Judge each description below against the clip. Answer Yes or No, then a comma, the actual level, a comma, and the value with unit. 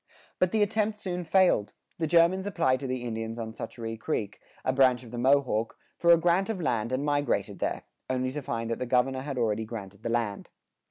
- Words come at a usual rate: No, fast, 215 wpm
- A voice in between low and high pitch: No, low, 130 Hz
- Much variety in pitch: Yes, wide, 6.6 semitones